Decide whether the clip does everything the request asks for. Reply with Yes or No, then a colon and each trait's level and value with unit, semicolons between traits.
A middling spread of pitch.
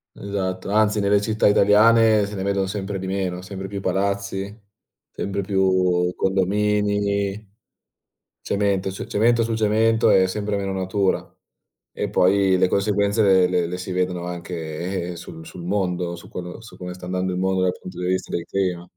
No: narrow, 1.9 semitones